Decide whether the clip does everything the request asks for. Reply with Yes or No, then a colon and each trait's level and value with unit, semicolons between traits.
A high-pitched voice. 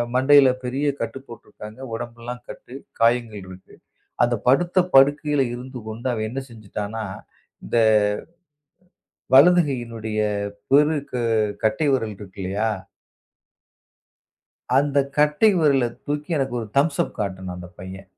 No: low, 125 Hz